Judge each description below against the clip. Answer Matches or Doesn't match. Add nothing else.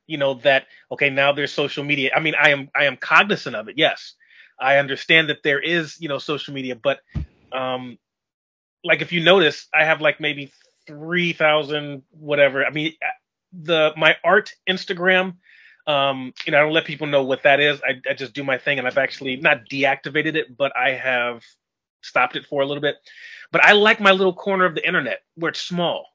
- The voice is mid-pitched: Matches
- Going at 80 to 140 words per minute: Doesn't match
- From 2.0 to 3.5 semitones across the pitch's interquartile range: Matches